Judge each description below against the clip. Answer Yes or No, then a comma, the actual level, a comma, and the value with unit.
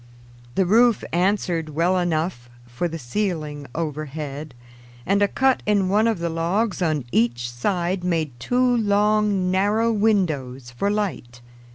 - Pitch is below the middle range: No, medium, 175 Hz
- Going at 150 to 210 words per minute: No, average, 140 wpm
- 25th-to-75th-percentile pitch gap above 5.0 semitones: Yes, wide, 5.4 semitones